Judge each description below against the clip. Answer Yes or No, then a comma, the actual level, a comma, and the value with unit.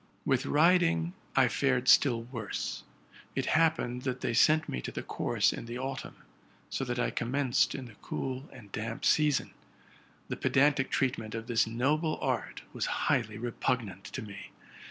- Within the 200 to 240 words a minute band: No, average, 160 wpm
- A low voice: Yes, low, 125 Hz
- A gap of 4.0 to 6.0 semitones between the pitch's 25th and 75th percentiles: No, average, 3.5 semitones